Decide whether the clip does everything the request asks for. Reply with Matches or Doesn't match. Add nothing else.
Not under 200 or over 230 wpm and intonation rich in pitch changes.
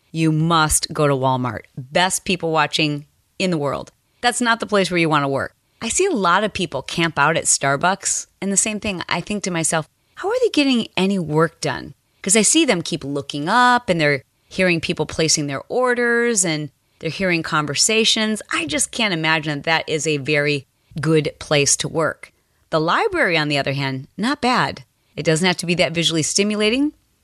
Matches